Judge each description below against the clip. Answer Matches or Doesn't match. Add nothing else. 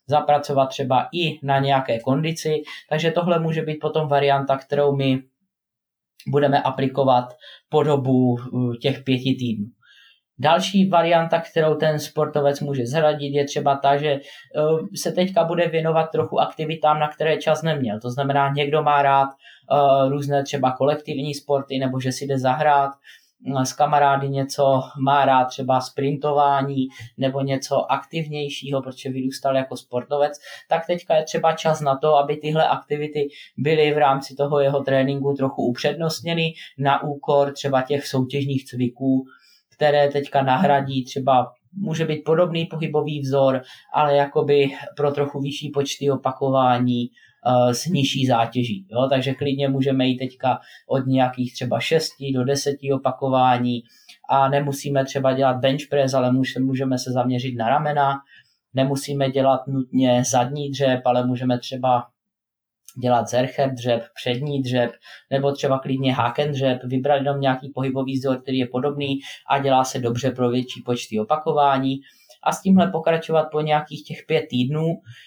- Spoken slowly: Doesn't match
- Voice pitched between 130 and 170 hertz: Matches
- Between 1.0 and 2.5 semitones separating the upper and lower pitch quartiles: Matches